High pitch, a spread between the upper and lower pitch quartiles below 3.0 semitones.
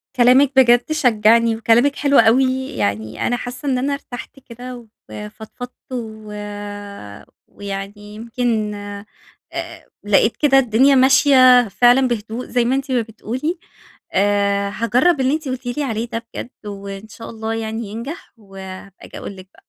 No: high, 235 Hz; average, 3.5 semitones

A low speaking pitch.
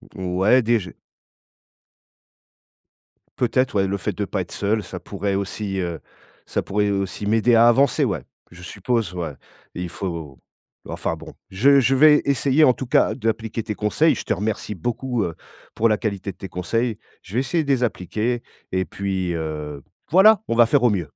Yes: low, 105 Hz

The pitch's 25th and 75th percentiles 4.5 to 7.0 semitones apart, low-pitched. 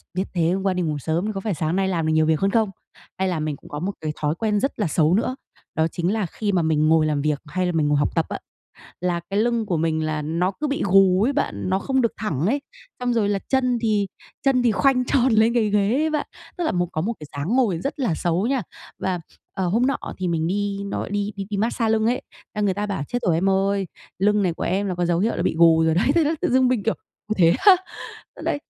No: average, 5.2 semitones; high, 195 Hz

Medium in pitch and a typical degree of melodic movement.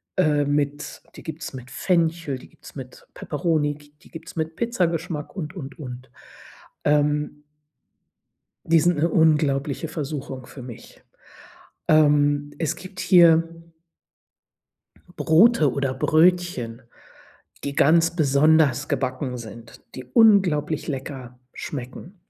Yes: medium, 150 Hz; average, 3.2 semitones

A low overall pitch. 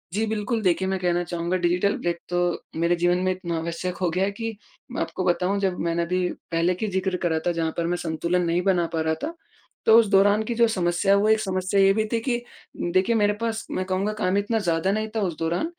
No: medium, 185 Hz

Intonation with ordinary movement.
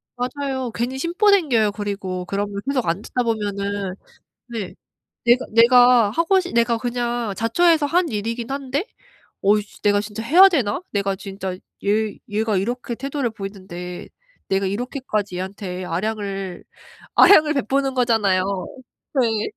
Yes: average, 4.3 semitones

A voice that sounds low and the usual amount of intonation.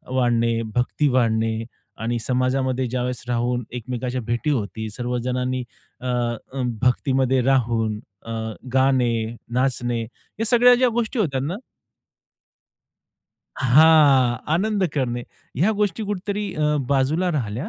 Yes: low, 130 Hz; average, 4.0 semitones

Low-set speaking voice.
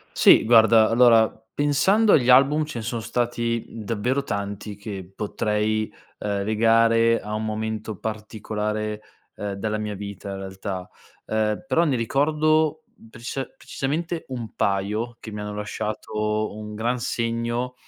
Yes: low, 110 Hz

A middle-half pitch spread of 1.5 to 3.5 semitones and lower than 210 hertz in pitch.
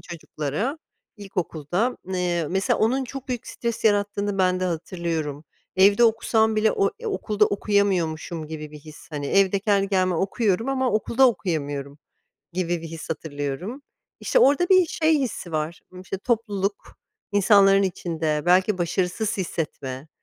No: average, 5.1 semitones; high, 190 Hz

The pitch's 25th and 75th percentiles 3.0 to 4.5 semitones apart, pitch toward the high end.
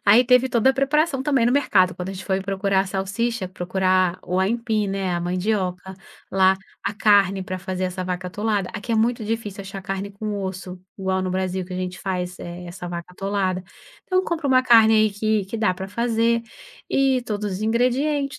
Yes: average, 3.6 semitones; high, 195 Hz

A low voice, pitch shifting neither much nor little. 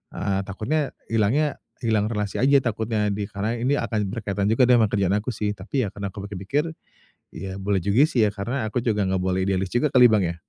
Yes: low, 105 Hz; average, 3.5 semitones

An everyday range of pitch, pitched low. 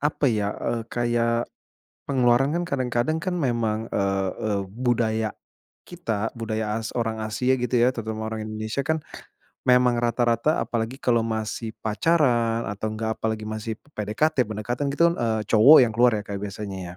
No: narrow, 2.3 semitones; low, 115 Hz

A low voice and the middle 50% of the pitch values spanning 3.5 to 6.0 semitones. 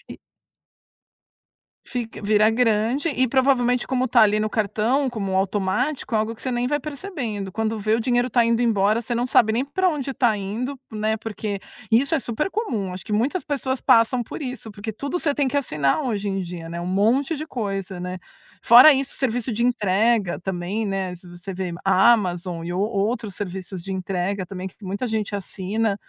No: high, 220 Hz; average, 4.4 semitones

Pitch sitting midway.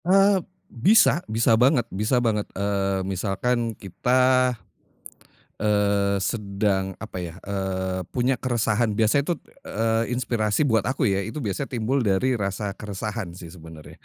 No: low, 110 Hz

